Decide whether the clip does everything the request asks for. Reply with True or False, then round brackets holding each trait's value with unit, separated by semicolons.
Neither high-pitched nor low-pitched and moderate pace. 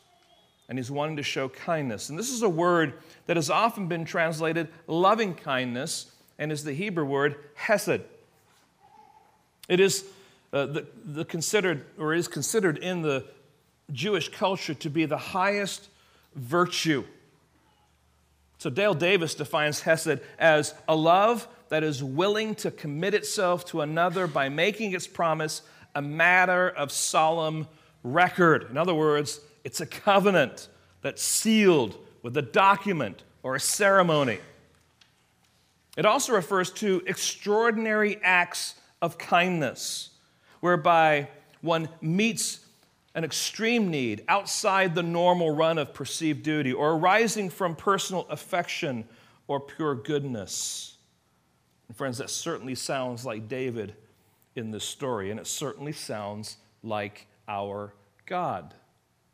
False (160 Hz; 130 wpm)